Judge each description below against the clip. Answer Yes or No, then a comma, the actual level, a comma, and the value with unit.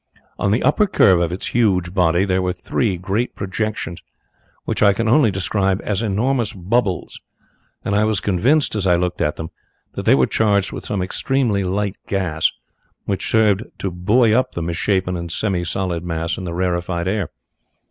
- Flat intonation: No, average, 3.3 semitones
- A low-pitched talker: Yes, very low, 95 Hz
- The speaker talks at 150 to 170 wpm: No, average, 180 wpm